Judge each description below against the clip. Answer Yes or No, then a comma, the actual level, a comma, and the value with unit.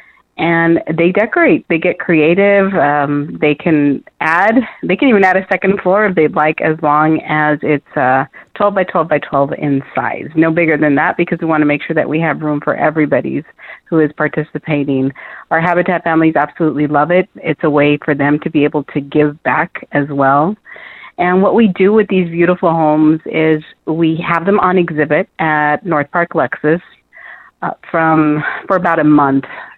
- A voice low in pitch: No, medium, 155 Hz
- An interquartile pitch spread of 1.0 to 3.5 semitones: Yes, average, 2.8 semitones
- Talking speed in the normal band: Yes, average, 190 wpm